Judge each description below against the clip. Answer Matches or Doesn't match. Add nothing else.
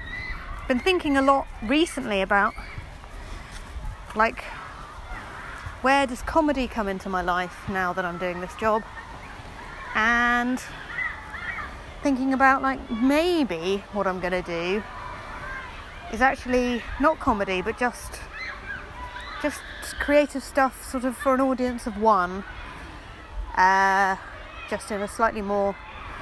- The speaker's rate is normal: Doesn't match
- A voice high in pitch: Matches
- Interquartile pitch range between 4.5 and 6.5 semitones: Matches